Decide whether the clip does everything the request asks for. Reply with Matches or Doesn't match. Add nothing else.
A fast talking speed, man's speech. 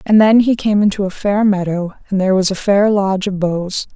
Doesn't match